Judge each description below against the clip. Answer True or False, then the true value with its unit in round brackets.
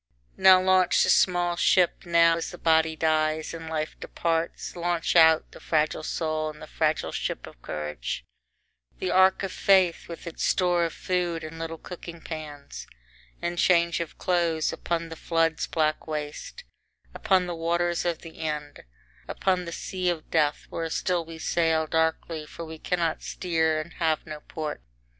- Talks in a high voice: False (165 Hz)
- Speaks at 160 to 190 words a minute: True (165 wpm)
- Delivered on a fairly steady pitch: True (1.7 semitones)